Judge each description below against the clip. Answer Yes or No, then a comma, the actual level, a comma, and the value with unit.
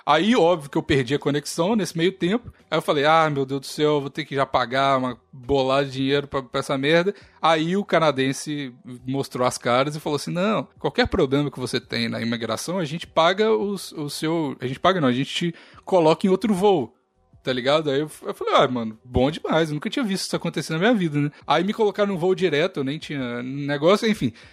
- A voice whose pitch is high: No, medium, 150 Hz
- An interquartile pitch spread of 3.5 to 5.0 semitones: Yes, average, 4.2 semitones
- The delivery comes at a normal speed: No, fast, 230 wpm